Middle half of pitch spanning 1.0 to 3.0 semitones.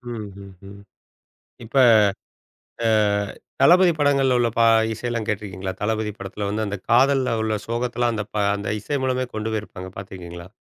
No: average, 3.4 semitones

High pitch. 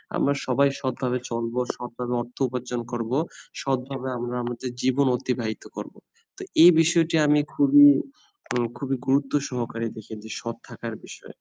No: low, 125 Hz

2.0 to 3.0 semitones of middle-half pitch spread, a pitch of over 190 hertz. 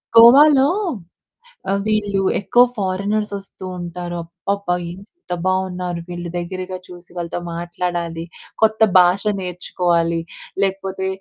No: narrow, 2.4 semitones; medium, 185 Hz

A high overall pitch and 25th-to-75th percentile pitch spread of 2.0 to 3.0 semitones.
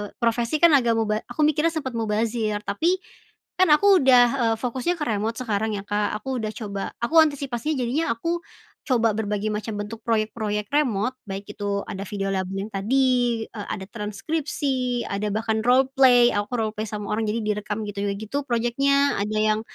No: high, 225 Hz; average, 3.7 semitones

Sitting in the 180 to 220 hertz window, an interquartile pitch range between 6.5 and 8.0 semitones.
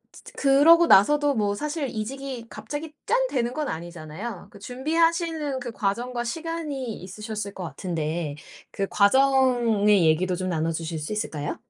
No: high, 230 Hz; wide, 7.1 semitones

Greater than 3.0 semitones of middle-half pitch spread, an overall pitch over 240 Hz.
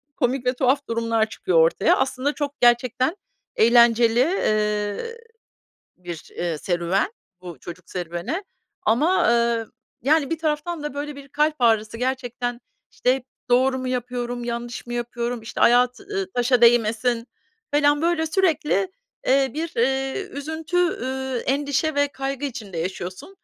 Yes: average, 3.8 semitones; very high, 250 Hz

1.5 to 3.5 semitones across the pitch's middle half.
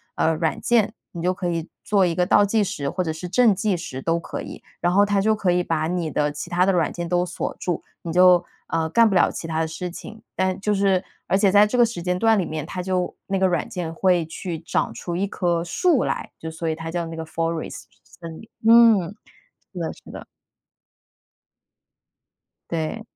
Yes: average, 3.0 semitones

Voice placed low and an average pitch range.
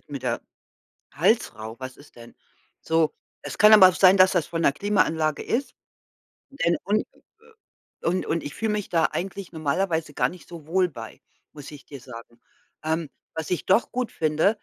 No: medium, 165 Hz; average, 4.7 semitones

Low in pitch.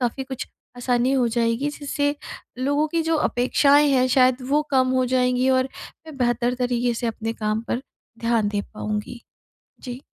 No: very high, 250 Hz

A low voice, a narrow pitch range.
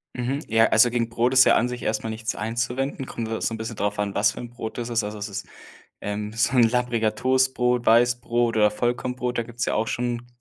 Yes: low, 120 Hz; narrow, 1.8 semitones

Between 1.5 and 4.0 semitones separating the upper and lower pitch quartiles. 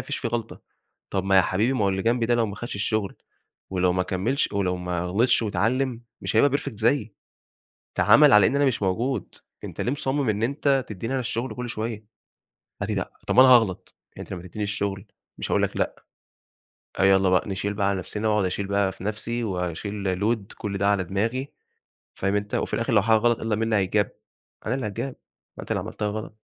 Yes: average, 3.4 semitones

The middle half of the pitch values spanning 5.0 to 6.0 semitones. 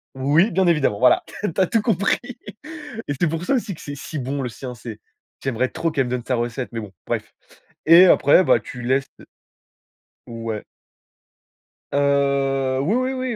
Yes: wide, 5.4 semitones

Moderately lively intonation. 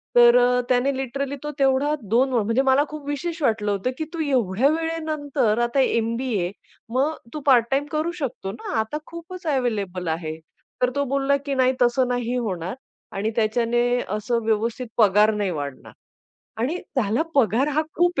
Yes: average, 4.2 semitones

